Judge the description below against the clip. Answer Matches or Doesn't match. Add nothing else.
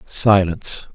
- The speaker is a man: Matches